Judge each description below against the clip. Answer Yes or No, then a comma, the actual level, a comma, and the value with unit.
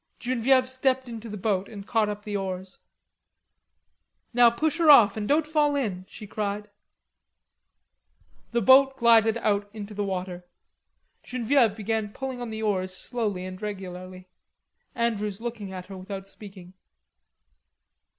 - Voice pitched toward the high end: Yes, high, 210 Hz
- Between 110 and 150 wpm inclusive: Yes, average, 140 wpm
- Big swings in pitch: No, average, 3.7 semitones